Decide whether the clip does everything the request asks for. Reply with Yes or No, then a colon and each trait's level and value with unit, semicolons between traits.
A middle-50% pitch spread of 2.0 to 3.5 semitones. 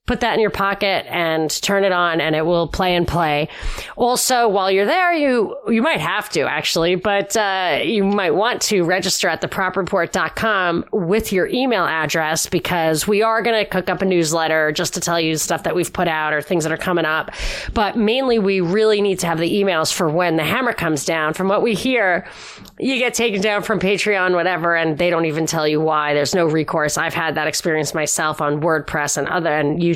No: average, 4.2 semitones